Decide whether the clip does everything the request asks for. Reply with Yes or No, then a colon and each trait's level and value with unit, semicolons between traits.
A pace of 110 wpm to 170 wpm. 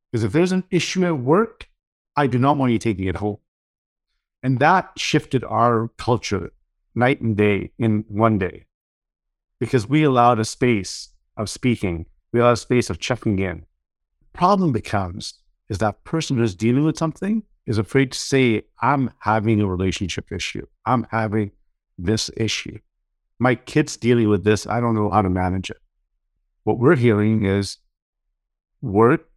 Yes: average, 160 wpm